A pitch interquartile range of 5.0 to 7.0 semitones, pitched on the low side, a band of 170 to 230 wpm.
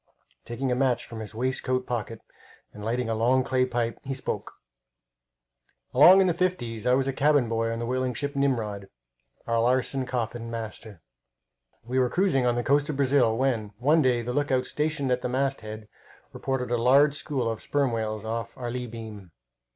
No: average, 2.9 semitones; low, 125 Hz; average, 180 wpm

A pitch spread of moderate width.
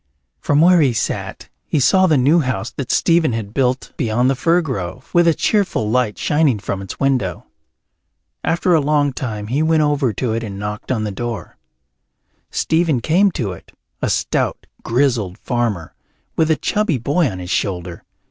No: wide, 6.4 semitones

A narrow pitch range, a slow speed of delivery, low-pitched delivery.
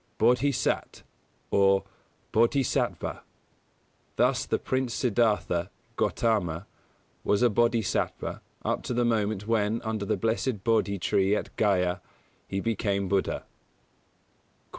No: average, 3.0 semitones; slow, 110 wpm; low, 110 Hz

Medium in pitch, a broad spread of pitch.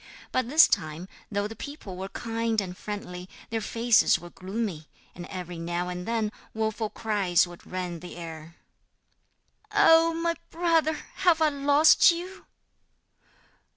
No: high, 210 Hz; wide, 8.0 semitones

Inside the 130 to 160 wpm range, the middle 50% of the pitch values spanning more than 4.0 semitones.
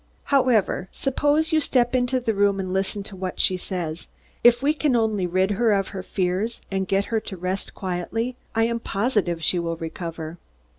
No: average, 190 wpm; average, 4.6 semitones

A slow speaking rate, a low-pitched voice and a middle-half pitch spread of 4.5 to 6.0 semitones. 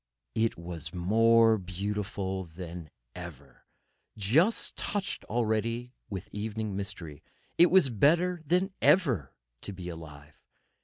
Yes: slow, 105 wpm; low, 105 Hz; wide, 5.5 semitones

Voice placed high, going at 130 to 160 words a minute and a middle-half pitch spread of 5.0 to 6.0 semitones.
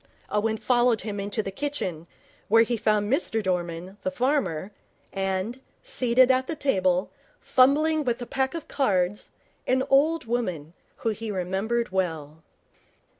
Yes: high, 220 Hz; average, 140 wpm; wide, 5.5 semitones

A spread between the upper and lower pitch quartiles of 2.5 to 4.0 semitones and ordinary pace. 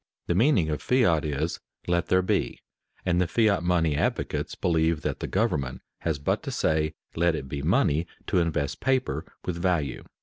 Yes: average, 2.9 semitones; average, 180 wpm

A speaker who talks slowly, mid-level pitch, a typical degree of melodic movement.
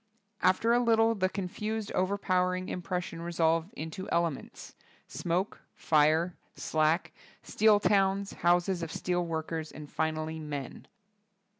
Yes: slow, 120 wpm; medium, 175 Hz; average, 3.4 semitones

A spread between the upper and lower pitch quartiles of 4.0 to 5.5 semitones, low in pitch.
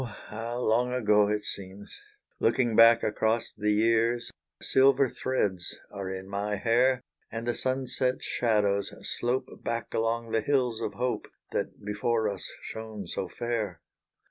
No: narrow, 2.5 semitones; low, 115 Hz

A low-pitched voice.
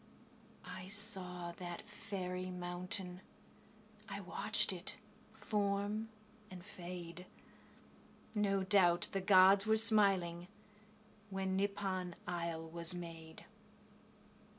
No: medium, 185 Hz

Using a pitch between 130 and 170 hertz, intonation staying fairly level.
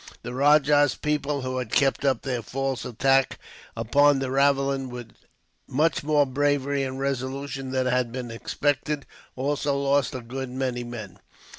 Yes: low, 135 Hz; narrow, 1.9 semitones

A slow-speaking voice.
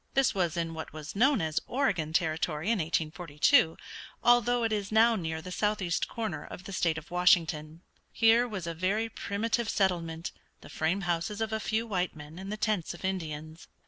No: average, 185 wpm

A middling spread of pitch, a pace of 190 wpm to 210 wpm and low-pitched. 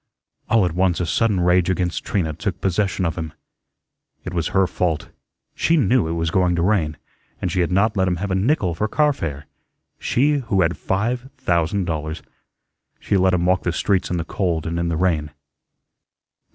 Yes: average, 3.1 semitones; average, 195 wpm; very low, 90 Hz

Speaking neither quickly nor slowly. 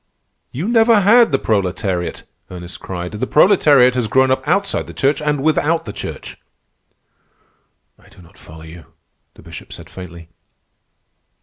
Yes: average, 145 wpm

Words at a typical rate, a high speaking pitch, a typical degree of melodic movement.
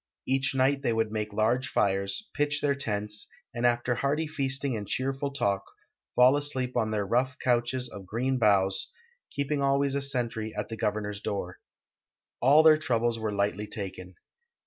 No: average, 165 wpm; low, 120 Hz; average, 4.5 semitones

